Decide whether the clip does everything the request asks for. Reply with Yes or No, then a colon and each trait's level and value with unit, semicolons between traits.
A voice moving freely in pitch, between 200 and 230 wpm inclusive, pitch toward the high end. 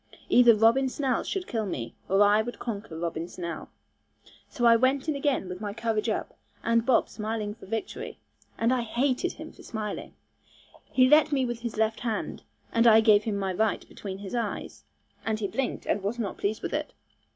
No: average, 3.1 semitones; fast, 205 wpm; high, 225 Hz